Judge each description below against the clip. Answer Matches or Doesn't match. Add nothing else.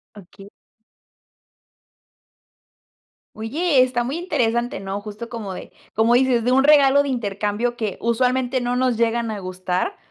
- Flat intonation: Doesn't match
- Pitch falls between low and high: Doesn't match